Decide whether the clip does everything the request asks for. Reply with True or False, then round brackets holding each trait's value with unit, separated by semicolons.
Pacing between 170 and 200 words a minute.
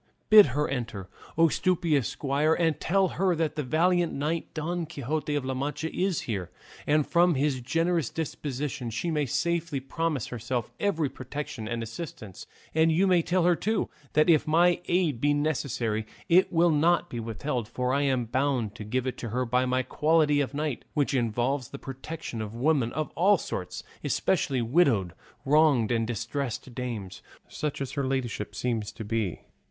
True (175 wpm)